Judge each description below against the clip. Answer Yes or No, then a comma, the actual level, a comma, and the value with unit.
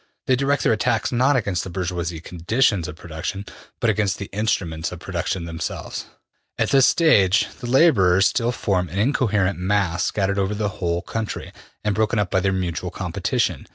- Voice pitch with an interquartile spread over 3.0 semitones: Yes, average, 3.8 semitones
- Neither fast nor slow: Yes, average, 175 wpm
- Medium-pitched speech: No, low, 100 Hz